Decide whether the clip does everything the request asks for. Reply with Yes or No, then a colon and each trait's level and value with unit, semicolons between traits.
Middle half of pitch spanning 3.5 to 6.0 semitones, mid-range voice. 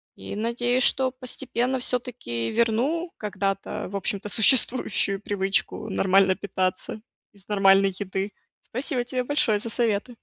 No: average, 4.2 semitones; high, 215 Hz